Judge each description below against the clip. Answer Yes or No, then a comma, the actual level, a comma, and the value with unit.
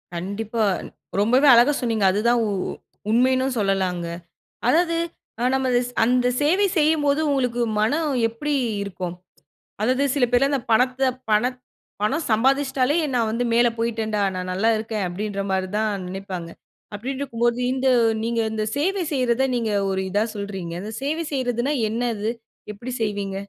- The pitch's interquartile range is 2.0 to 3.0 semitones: No, average, 4.3 semitones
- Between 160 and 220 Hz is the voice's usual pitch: No, high, 235 Hz